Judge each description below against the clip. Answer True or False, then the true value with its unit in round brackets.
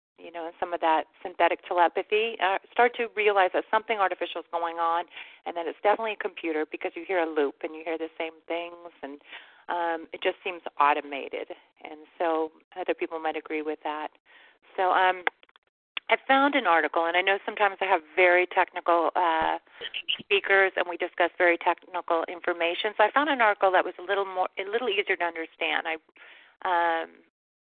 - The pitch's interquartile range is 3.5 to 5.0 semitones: False (3.0 semitones)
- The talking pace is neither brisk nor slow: True (190 wpm)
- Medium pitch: True (175 Hz)